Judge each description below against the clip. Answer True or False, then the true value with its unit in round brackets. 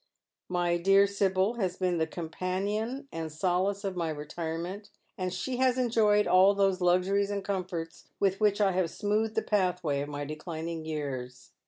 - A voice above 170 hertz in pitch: True (185 Hz)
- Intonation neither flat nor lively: True (3.5 semitones)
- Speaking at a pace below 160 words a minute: False (165 wpm)